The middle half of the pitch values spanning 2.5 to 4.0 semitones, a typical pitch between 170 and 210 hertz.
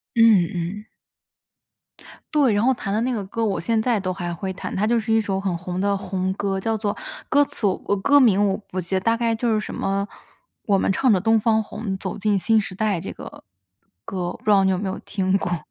Yes: average, 2.8 semitones; high, 200 Hz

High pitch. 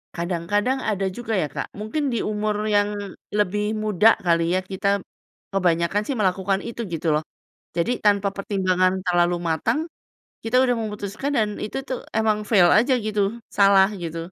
Yes: high, 200 Hz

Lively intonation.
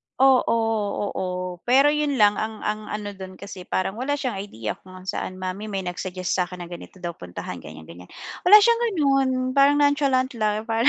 Yes: wide, 6.4 semitones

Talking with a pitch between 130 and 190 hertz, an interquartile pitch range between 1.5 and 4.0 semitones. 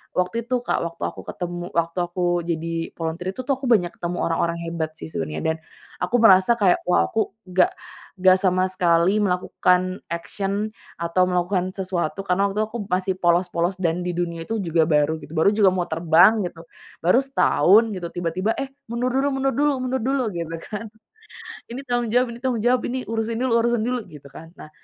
No: medium, 185 Hz; average, 4.9 semitones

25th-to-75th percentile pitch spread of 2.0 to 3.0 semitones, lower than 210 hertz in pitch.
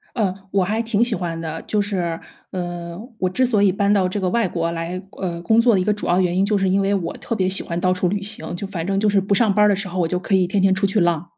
Yes: average, 2.7 semitones; high, 190 Hz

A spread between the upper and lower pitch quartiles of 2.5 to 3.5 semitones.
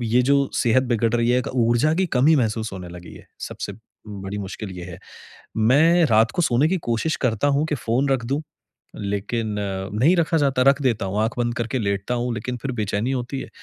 No: average, 4.2 semitones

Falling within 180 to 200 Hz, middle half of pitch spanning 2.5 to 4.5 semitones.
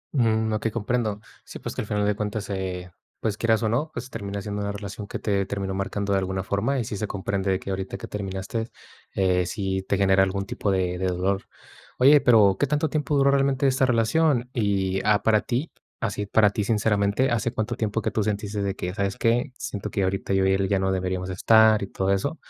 No: low, 105 Hz; average, 2.9 semitones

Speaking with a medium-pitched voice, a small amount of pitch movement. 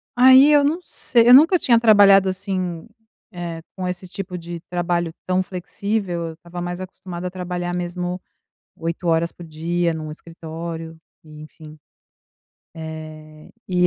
Yes: medium, 175 Hz; narrow, 2.2 semitones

